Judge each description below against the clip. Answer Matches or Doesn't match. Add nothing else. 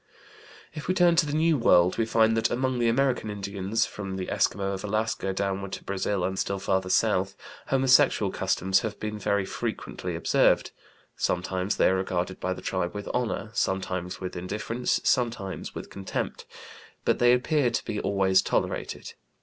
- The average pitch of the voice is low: Matches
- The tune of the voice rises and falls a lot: Doesn't match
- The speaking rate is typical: Matches